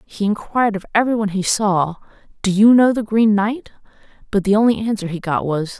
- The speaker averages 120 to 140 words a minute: No, average, 195 wpm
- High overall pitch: Yes, high, 205 Hz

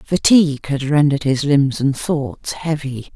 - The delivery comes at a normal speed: Yes, average, 150 wpm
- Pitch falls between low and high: Yes, medium, 145 Hz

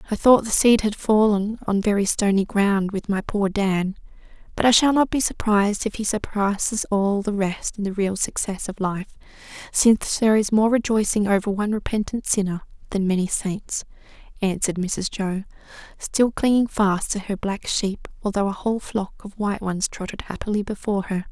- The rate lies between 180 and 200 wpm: Yes, average, 185 wpm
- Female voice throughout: Yes, female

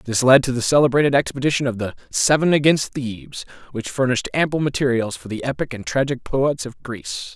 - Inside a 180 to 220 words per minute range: Yes, average, 190 wpm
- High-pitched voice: No, low, 130 Hz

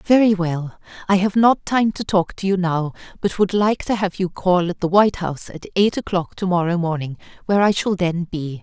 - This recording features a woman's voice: Yes, female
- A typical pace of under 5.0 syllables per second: No, 5.3 syllables/s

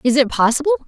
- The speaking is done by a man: No, female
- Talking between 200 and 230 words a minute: Yes, fast, 205 wpm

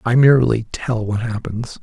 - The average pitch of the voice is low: Yes, low, 115 Hz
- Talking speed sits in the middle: Yes, average, 165 wpm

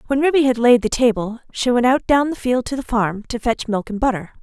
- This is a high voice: Yes, high, 245 Hz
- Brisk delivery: Yes, fast, 270 wpm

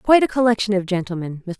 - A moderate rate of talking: Yes, average, 190 wpm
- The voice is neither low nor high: No, high, 205 Hz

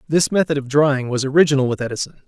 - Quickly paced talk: Yes, fast, 210 wpm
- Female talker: No, male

